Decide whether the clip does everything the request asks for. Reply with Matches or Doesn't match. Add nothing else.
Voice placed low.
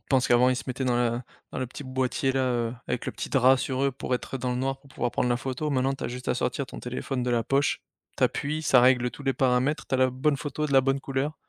Matches